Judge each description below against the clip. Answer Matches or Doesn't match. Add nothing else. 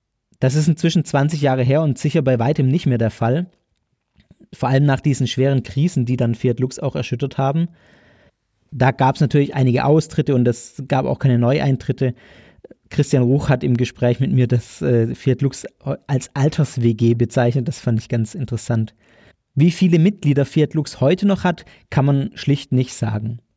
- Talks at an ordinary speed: Matches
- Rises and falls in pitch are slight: Doesn't match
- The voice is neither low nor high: Doesn't match